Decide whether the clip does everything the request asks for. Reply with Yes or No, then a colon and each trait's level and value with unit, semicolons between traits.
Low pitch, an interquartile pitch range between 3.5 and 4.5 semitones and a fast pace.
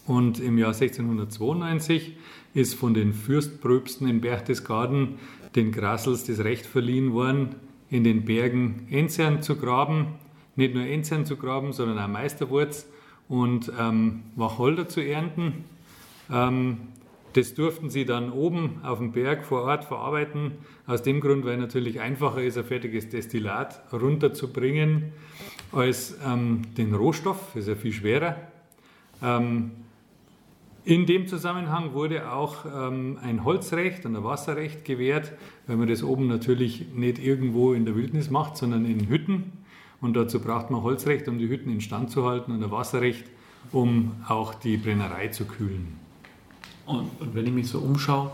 No: low, 130 Hz; average, 3.9 semitones; average, 150 wpm